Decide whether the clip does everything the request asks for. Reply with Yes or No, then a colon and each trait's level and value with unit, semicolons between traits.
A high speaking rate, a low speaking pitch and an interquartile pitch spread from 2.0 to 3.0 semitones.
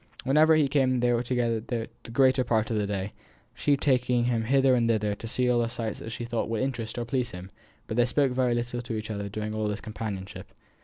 Yes: fast, 240 wpm; low, 120 Hz; narrow, 2.6 semitones